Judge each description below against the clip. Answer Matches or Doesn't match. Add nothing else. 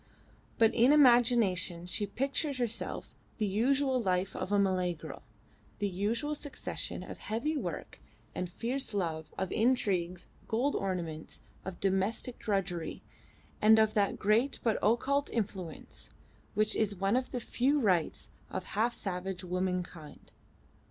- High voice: Matches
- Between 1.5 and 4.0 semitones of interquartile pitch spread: Doesn't match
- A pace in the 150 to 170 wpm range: Doesn't match